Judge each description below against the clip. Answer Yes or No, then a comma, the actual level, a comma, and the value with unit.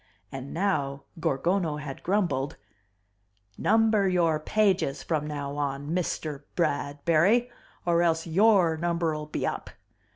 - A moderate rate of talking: No, slow, 110 wpm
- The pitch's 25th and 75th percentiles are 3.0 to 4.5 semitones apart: Yes, average, 4.2 semitones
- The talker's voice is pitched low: No, medium, 165 Hz